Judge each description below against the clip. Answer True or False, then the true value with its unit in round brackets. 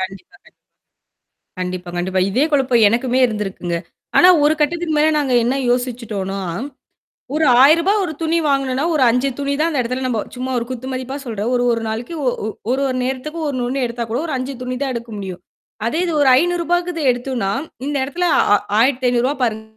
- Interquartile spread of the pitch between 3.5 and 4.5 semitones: True (4.0 semitones)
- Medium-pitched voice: False (255 Hz)